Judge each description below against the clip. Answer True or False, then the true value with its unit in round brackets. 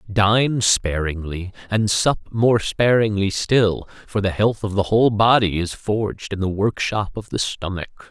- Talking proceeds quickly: False (165 wpm)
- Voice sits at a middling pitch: False (105 Hz)